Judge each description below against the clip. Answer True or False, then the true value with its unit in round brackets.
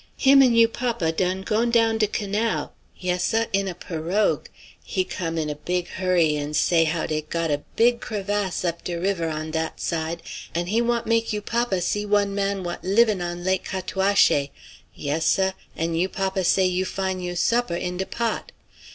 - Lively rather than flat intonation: False (3.7 semitones)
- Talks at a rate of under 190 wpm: False (195 wpm)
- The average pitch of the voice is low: False (185 Hz)